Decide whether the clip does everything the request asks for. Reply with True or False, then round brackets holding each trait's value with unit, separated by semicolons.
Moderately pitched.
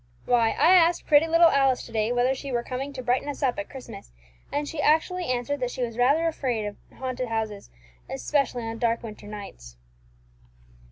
False (255 Hz)